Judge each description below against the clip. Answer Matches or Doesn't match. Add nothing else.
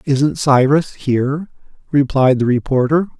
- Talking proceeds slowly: Matches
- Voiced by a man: Matches